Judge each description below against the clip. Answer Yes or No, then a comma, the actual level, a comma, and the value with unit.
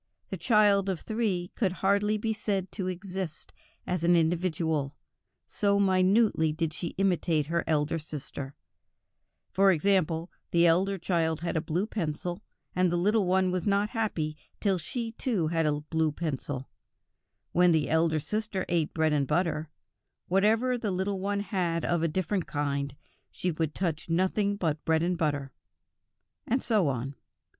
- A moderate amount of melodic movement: Yes, average, 3.7 semitones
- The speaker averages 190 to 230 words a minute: No, average, 155 wpm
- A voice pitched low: No, medium, 175 Hz